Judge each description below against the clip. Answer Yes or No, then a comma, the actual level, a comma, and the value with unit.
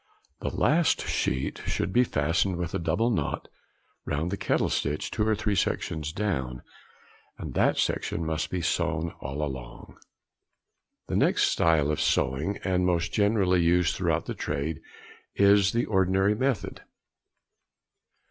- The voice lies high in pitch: No, very low, 90 Hz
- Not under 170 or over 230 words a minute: No, average, 140 wpm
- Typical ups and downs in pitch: Yes, average, 4.5 semitones